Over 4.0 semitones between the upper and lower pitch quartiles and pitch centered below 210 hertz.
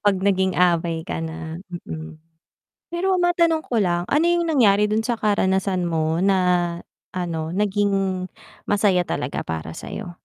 No: average, 3.7 semitones; high, 190 Hz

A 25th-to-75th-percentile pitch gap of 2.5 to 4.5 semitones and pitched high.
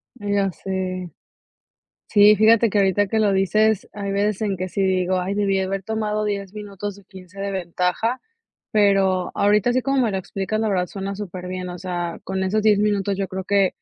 No: narrow, 1.9 semitones; high, 195 Hz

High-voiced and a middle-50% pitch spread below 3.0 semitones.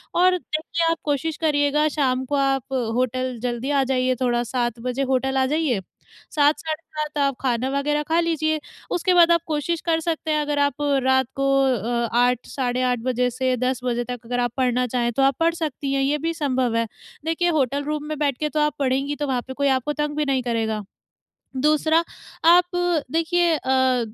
No: very high, 275 Hz; average, 3.4 semitones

